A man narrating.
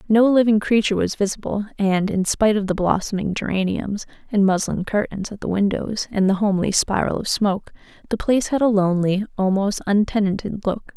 No: female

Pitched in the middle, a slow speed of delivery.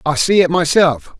No: medium, 165 Hz; average, 200 wpm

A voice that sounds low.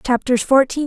No: very high, 260 Hz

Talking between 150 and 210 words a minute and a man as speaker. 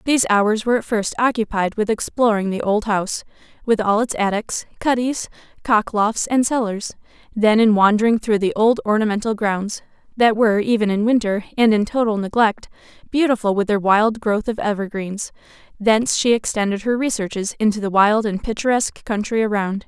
No: average, 170 wpm; female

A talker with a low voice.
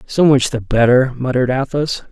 Yes: low, 130 Hz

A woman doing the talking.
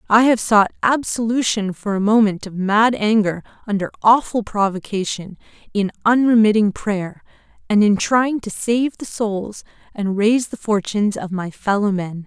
Yes: female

